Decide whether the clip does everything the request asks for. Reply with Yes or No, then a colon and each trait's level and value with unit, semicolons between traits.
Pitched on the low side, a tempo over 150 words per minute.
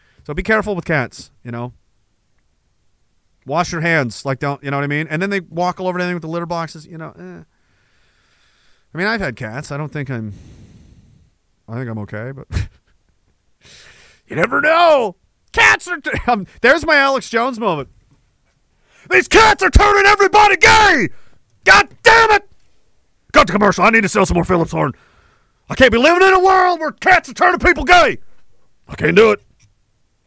No: medium, 175 Hz; average, 185 wpm